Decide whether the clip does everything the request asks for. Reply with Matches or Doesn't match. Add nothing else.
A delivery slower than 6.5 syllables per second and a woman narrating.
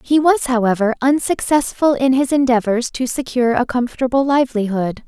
Matches